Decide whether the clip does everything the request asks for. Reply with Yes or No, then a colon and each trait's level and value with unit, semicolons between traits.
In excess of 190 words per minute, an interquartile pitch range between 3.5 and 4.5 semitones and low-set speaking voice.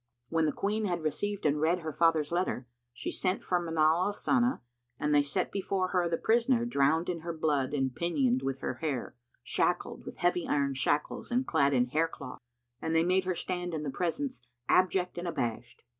No: average, 200 wpm; average, 4.1 semitones; medium, 165 Hz